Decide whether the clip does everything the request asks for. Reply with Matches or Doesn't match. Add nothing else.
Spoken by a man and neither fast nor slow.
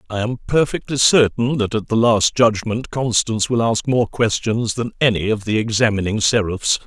Matches